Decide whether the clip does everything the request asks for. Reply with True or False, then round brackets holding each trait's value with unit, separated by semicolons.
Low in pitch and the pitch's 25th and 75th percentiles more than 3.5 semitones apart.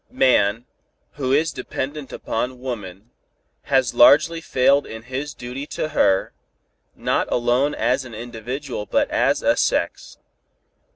False (130 Hz; 2.9 semitones)